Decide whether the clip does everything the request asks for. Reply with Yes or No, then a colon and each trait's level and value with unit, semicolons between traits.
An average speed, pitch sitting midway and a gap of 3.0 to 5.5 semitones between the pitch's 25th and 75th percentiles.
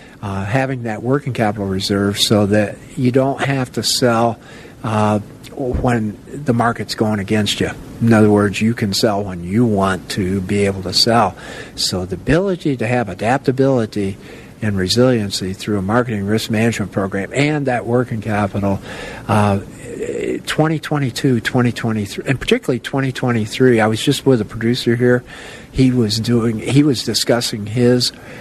No: average, 150 wpm; low, 115 Hz; average, 3.5 semitones